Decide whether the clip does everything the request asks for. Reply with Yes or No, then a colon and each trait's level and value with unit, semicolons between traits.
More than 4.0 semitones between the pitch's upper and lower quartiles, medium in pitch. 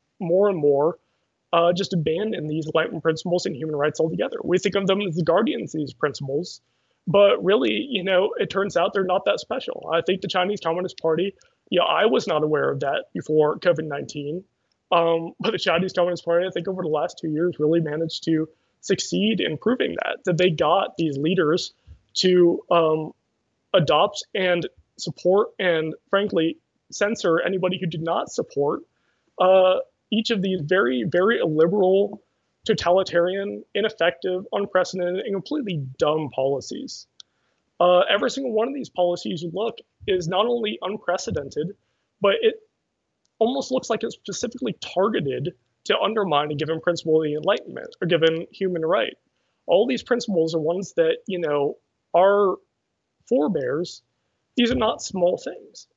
No: average, 3.5 semitones; medium, 180 Hz